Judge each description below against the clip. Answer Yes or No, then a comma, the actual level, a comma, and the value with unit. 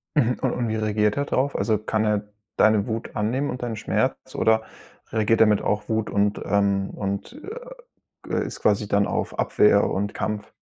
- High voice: No, low, 110 Hz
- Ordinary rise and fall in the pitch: No, narrow, 1.7 semitones